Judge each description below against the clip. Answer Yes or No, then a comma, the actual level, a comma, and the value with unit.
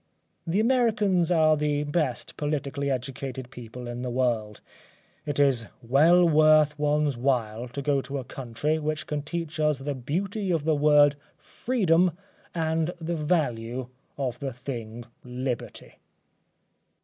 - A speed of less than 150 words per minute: Yes, slow, 135 wpm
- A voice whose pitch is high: No, medium, 145 Hz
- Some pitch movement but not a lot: Yes, average, 4.0 semitones